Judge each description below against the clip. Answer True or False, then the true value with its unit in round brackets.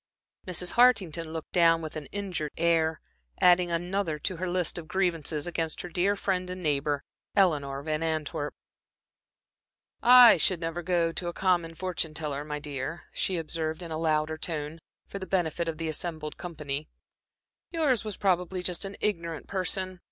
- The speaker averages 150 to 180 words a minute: True (165 wpm)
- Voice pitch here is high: False (170 Hz)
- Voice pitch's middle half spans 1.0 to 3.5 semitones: True (2.8 semitones)